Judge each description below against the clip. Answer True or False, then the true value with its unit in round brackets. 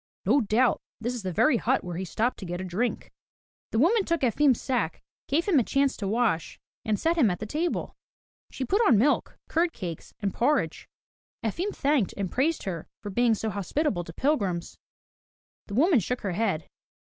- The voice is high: True (235 Hz)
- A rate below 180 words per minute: False (195 wpm)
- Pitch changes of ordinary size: False (6.7 semitones)